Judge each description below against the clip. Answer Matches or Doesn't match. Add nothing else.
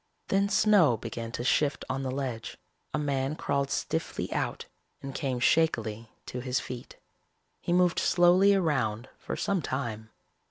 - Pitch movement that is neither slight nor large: Doesn't match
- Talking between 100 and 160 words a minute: Matches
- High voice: Doesn't match